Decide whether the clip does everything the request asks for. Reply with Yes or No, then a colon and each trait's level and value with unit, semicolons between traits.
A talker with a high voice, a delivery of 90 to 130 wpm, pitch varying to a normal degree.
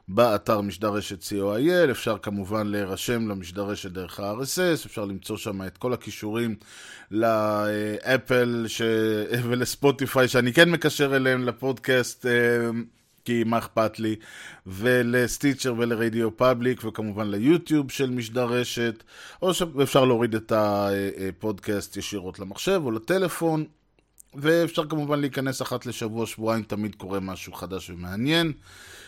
No: low, 115 Hz; average, 110 wpm; average, 3.7 semitones